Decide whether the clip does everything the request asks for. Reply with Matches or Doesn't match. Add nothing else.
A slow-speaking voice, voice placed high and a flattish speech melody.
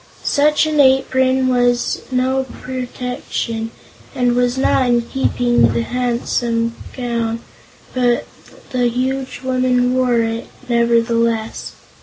Matches